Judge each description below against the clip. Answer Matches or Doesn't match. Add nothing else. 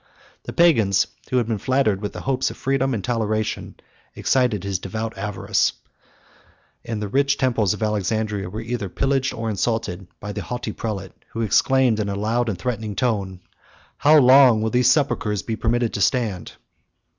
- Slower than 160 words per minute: Doesn't match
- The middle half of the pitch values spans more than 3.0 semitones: Matches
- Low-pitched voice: Matches